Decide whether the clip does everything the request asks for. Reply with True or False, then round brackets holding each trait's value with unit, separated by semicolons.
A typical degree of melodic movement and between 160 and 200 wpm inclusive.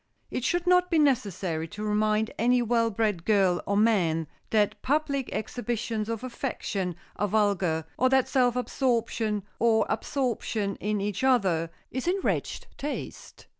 False (4.0 semitones; 145 wpm)